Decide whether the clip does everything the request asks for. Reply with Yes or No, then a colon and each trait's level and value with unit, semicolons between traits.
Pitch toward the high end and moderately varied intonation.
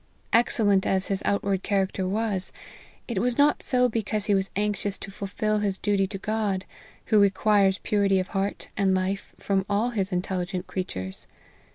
No: high, 200 Hz; narrow, 1.8 semitones